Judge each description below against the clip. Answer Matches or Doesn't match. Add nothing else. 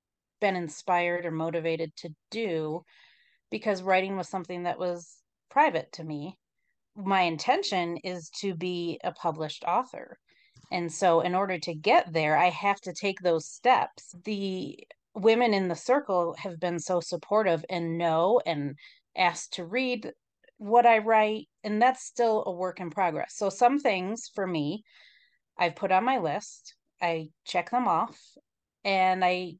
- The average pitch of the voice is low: Doesn't match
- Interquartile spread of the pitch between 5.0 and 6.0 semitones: Doesn't match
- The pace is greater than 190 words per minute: Doesn't match